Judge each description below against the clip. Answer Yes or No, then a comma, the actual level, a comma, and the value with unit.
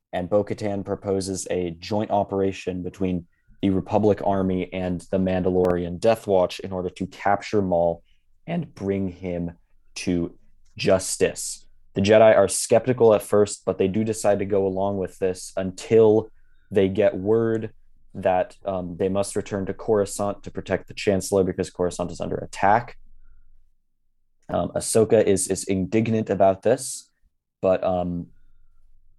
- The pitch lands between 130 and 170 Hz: No, very low, 95 Hz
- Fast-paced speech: No, average, 140 wpm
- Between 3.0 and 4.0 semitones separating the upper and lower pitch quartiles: No, narrow, 2.4 semitones